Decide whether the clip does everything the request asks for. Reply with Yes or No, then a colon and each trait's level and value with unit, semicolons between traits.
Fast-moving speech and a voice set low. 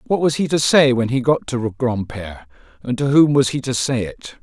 Yes: fast, 245 wpm; low, 125 Hz